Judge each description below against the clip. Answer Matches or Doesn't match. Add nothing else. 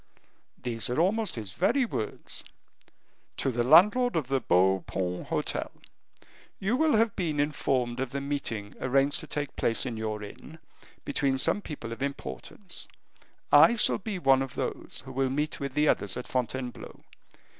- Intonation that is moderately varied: Matches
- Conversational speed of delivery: Matches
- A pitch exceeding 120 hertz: Matches